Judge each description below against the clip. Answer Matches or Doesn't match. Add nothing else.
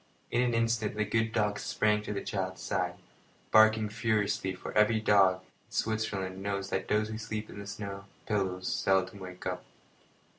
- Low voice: Matches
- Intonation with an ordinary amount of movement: Doesn't match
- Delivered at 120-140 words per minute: Doesn't match